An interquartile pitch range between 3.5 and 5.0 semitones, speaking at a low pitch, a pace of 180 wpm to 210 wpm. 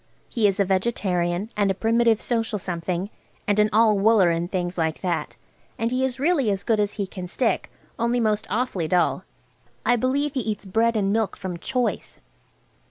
No: average, 3.8 semitones; high, 210 Hz; average, 185 wpm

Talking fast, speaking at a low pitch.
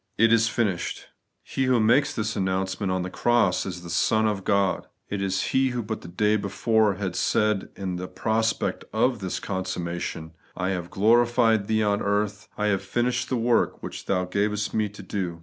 Yes: fast, 210 wpm; low, 105 Hz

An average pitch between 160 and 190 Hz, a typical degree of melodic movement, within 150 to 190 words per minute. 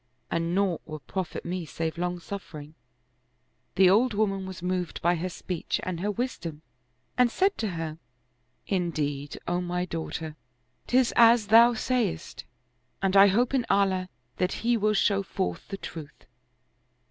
Yes: medium, 185 Hz; average, 4.0 semitones; average, 155 wpm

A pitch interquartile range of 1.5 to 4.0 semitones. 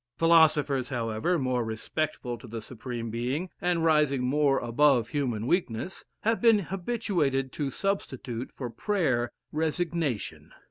No: wide, 5.5 semitones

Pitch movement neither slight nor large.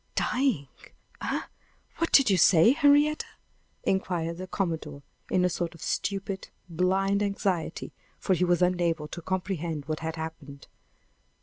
Yes: average, 3.3 semitones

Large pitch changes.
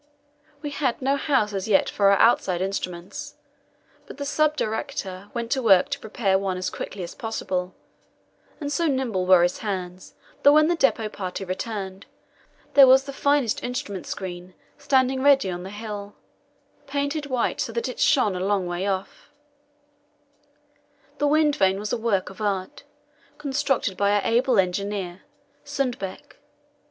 Yes: wide, 6.2 semitones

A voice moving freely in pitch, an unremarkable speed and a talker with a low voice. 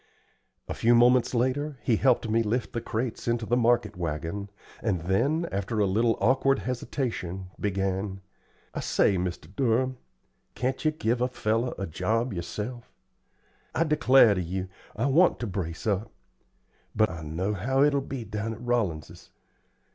No: average, 4.7 semitones; average, 155 wpm; low, 115 Hz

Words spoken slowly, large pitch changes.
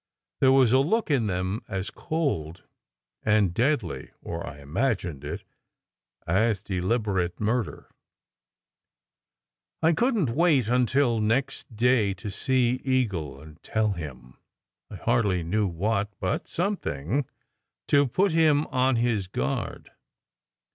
Yes: slow, 120 wpm; wide, 6.2 semitones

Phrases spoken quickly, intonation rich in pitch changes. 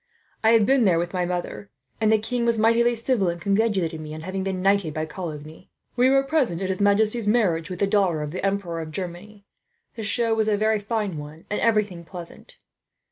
No: fast, 215 wpm; average, 4.4 semitones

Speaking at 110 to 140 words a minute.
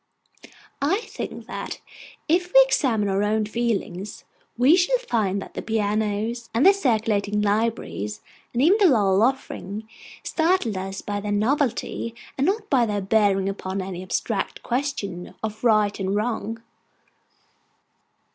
Yes: slow, 135 wpm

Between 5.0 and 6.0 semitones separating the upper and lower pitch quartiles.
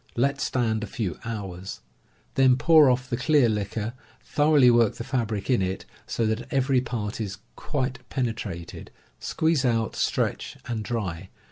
No: average, 3.7 semitones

